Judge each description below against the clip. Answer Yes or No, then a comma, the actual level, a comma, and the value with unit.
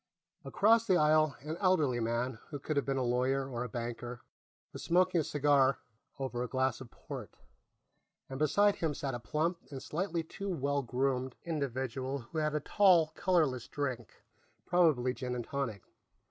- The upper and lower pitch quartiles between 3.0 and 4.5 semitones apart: Yes, average, 4.1 semitones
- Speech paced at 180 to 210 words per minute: No, average, 170 wpm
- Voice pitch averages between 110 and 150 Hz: Yes, medium, 140 Hz